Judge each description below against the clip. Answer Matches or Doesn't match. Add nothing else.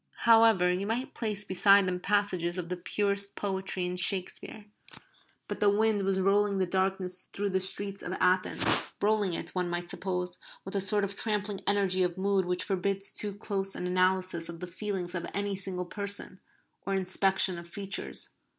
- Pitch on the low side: Doesn't match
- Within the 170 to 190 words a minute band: Matches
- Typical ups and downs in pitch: Doesn't match